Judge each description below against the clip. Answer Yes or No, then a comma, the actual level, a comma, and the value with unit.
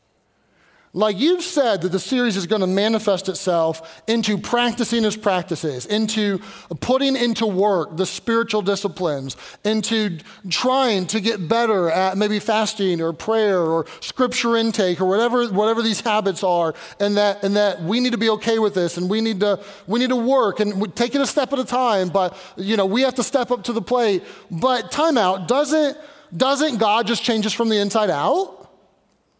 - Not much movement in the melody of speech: No, average, 3.7 semitones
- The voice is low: No, high, 215 Hz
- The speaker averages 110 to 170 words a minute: No, average, 185 wpm